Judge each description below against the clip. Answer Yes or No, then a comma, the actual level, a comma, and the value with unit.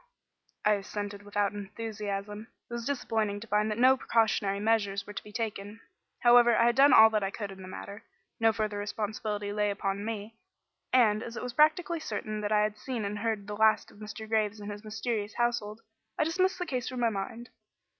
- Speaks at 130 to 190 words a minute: No, fast, 205 wpm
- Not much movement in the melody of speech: Yes, narrow, 2.2 semitones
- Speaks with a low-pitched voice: No, high, 215 Hz